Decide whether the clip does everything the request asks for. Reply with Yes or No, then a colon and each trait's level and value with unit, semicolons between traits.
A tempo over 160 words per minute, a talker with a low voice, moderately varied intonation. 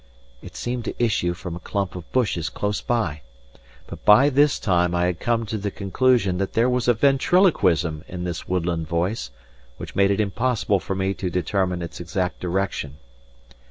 Yes: average, 180 wpm; very low, 95 Hz; average, 4.7 semitones